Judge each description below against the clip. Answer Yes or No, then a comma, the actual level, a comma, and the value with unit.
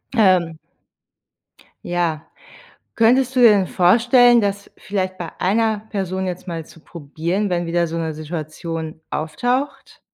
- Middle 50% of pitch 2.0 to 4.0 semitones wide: No, average, 4.7 semitones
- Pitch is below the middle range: No, medium, 185 Hz